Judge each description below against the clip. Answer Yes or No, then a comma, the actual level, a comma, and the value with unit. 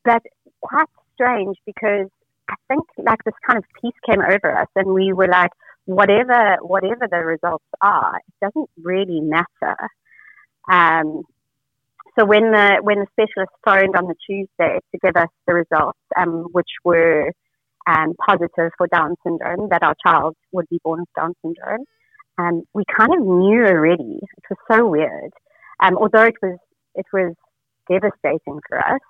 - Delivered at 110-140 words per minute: No, average, 165 wpm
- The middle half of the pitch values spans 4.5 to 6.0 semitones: No, average, 4.1 semitones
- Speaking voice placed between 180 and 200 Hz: Yes, medium, 185 Hz